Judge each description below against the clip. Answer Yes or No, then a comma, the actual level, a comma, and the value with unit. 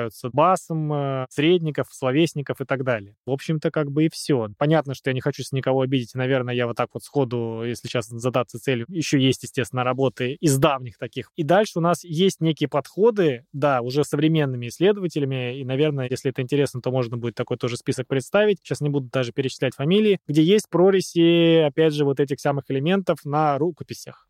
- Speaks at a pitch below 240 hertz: Yes, medium, 140 Hz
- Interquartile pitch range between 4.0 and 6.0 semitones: No, average, 3.6 semitones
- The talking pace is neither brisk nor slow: No, fast, 190 wpm